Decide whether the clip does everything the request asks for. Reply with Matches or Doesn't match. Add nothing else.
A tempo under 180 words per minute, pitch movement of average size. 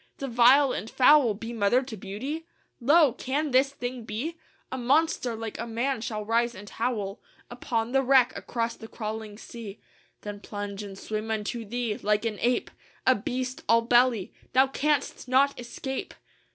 Matches